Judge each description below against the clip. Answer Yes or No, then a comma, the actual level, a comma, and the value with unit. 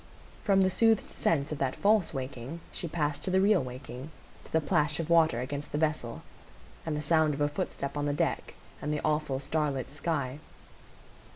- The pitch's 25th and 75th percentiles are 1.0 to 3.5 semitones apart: Yes, average, 2.9 semitones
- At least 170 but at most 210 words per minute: Yes, average, 185 wpm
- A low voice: No, medium, 150 Hz